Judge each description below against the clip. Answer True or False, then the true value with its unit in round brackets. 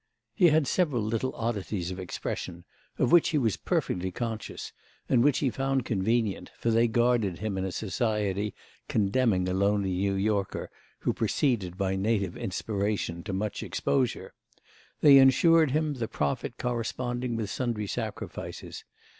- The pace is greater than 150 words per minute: False (145 wpm)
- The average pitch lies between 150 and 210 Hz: False (110 Hz)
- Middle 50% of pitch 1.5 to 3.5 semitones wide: False (4.2 semitones)